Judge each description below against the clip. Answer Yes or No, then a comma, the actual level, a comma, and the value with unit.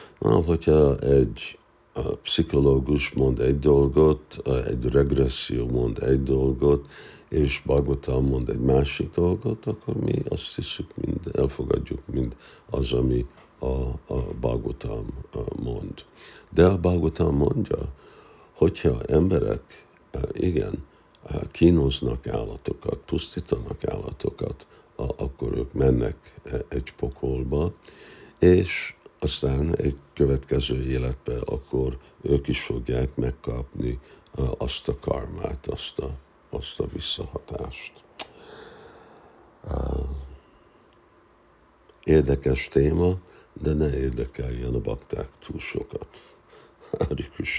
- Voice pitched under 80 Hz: Yes, very low, 70 Hz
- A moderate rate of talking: No, slow, 95 wpm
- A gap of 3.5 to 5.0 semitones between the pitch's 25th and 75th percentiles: No, average, 2.9 semitones